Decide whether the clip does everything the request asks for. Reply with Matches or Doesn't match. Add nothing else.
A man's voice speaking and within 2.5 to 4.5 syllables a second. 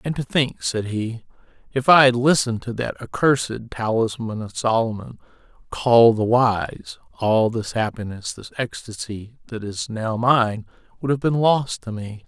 Matches